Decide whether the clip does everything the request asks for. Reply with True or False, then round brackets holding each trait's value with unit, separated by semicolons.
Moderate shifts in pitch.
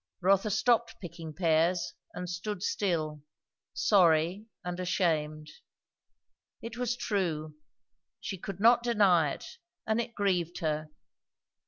True (4.5 semitones)